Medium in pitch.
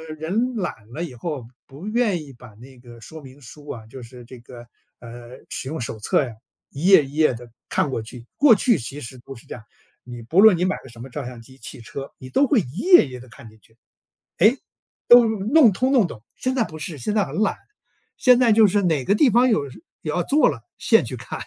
Yes: medium, 145 Hz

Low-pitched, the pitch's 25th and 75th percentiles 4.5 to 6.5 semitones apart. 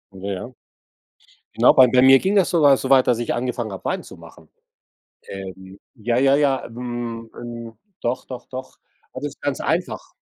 No: low, 125 Hz; average, 2.7 semitones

